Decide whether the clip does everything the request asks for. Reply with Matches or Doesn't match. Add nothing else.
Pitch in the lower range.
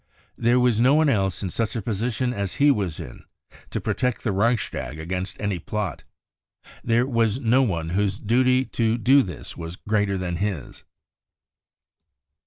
Matches